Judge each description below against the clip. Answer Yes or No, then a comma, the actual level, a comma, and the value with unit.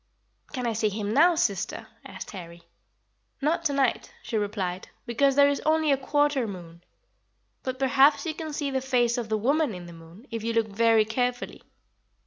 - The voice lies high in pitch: Yes, high, 240 Hz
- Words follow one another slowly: No, average, 185 wpm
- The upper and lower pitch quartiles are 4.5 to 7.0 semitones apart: Yes, average, 5.1 semitones